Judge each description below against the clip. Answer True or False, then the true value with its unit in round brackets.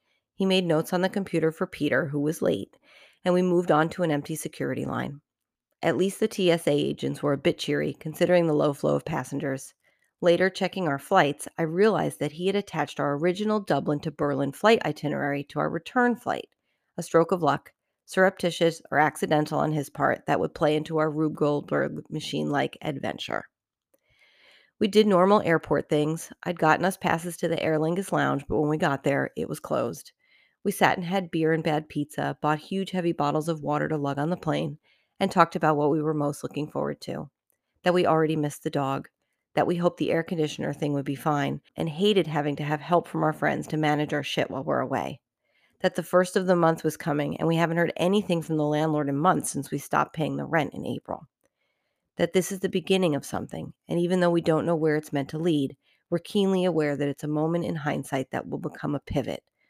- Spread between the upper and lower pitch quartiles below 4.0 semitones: True (3.3 semitones)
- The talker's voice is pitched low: False (160 Hz)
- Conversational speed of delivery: False (220 wpm)